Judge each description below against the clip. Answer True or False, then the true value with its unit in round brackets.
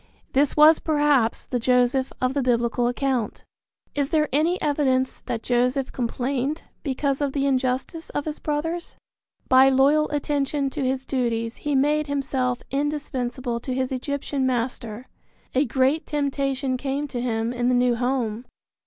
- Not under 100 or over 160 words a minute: True (150 wpm)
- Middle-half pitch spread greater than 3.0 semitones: False (2.6 semitones)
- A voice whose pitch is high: True (265 Hz)